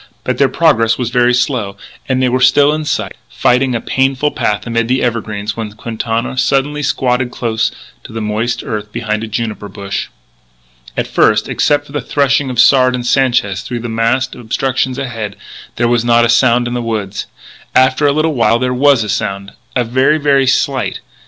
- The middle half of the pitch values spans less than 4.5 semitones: Yes, average, 2.7 semitones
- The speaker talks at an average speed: Yes, average, 185 wpm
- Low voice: Yes, low, 120 Hz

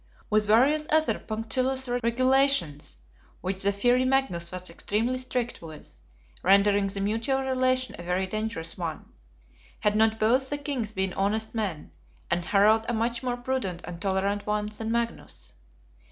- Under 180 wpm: Yes, average, 150 wpm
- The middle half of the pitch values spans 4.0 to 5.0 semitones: Yes, average, 4.6 semitones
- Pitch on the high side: Yes, high, 220 Hz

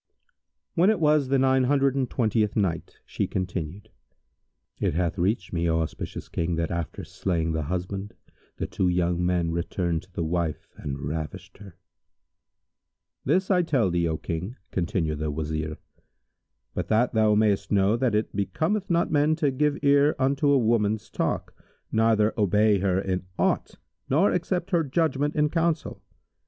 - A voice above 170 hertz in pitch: No, low, 105 Hz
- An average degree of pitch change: No, wide, 8.2 semitones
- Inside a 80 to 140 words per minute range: No, average, 160 wpm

